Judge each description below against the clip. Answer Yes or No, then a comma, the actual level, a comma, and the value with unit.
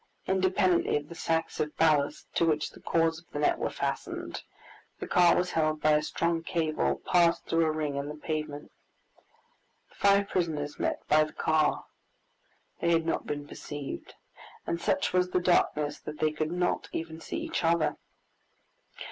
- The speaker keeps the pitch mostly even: Yes, narrow, 2.2 semitones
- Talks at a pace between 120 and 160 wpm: No, average, 175 wpm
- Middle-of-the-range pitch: Yes, medium, 160 Hz